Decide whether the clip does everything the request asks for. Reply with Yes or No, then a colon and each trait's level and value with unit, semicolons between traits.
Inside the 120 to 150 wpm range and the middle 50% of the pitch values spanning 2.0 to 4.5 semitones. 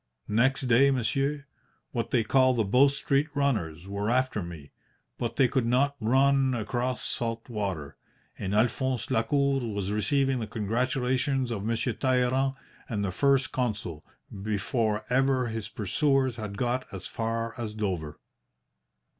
Yes: average, 140 wpm; average, 3.8 semitones